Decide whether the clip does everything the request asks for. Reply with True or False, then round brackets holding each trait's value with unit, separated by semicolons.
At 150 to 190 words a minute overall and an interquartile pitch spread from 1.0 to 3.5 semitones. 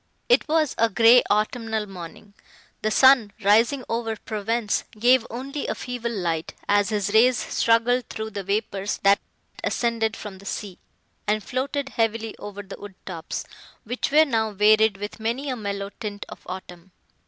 True (160 wpm; 2.8 semitones)